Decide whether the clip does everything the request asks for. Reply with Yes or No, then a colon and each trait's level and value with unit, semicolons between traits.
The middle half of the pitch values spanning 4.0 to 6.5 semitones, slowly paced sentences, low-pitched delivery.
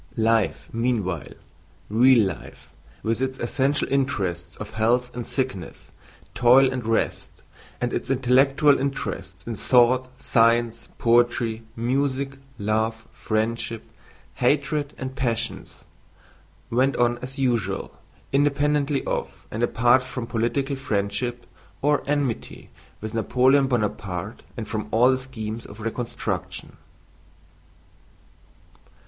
No: average, 3.1 semitones; slow, 105 wpm; low, 120 Hz